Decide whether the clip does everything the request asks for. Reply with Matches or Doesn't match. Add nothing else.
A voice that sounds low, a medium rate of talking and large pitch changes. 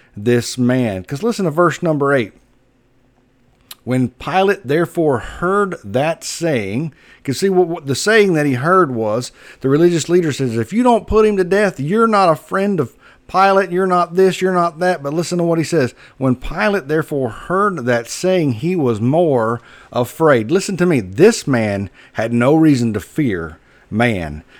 Doesn't match